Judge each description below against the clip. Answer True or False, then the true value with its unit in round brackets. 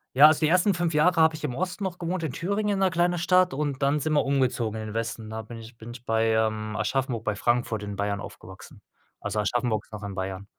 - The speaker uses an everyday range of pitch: False (7.2 semitones)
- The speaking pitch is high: False (125 Hz)